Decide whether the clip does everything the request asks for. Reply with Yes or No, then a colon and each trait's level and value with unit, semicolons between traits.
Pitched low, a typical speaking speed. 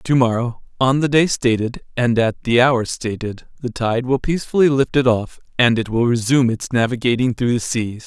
Yes: low, 125 Hz; average, 195 wpm